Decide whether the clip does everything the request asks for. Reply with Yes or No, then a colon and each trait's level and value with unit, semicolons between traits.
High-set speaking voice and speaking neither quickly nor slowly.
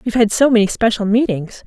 No: high, 220 Hz; fast, 215 wpm